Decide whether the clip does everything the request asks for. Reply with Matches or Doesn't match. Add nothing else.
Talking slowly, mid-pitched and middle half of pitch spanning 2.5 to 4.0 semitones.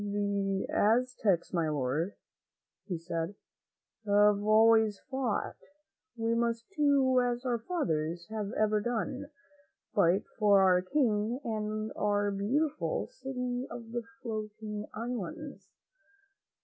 Doesn't match